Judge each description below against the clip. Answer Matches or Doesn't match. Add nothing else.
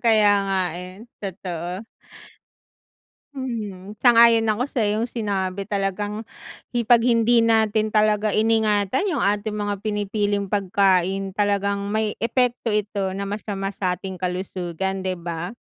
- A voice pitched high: Matches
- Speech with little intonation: Matches